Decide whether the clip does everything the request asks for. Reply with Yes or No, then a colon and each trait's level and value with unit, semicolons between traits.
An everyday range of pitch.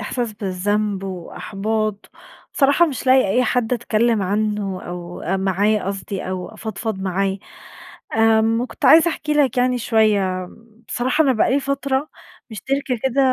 Yes: average, 4.7 semitones